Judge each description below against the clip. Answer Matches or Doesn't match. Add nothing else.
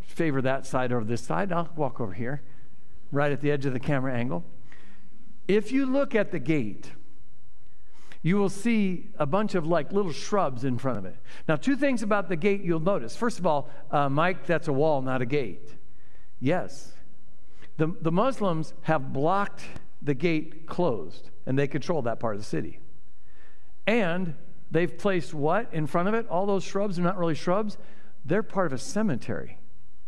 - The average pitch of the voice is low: Doesn't match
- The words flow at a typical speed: Matches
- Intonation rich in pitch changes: Matches